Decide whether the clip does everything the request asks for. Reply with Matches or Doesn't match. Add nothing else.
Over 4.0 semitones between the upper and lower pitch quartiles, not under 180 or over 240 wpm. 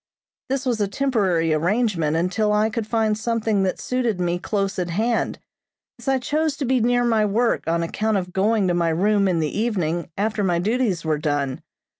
Matches